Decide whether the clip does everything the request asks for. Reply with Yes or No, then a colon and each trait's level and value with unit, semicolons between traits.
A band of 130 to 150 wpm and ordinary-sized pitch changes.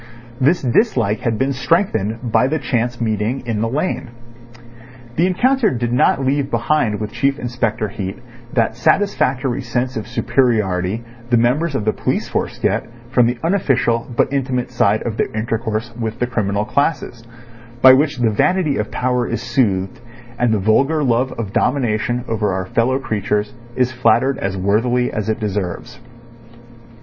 No: average, 160 wpm; average, 3.4 semitones